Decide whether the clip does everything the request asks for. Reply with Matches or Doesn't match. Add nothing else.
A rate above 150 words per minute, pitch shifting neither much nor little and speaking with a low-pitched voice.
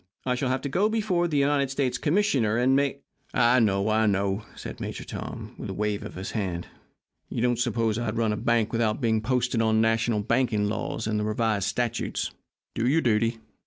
Matches